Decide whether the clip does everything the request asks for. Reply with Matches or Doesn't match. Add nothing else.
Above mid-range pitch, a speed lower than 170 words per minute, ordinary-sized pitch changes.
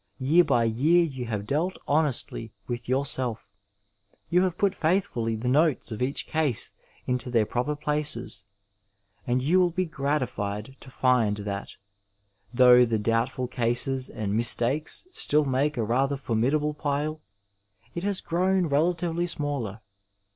Doesn't match